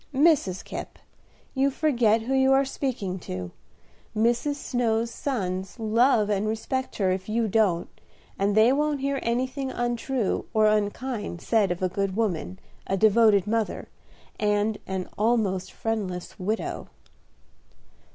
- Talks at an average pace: No, slow, 130 wpm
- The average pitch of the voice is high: Yes, high, 220 Hz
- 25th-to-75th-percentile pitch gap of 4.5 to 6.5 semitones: No, average, 4.0 semitones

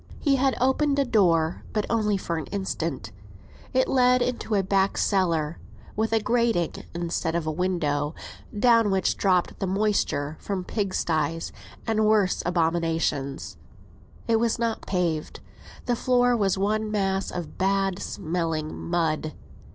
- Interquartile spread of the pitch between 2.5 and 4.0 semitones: No, average, 4.9 semitones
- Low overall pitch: No, high, 190 Hz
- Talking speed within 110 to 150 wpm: Yes, average, 140 wpm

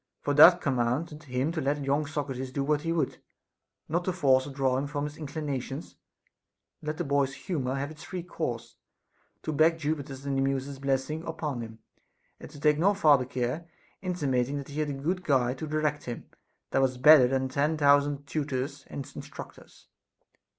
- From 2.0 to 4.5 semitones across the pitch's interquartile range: Yes, narrow, 2.5 semitones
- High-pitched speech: No, medium, 145 Hz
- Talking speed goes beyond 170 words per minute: Yes, average, 185 wpm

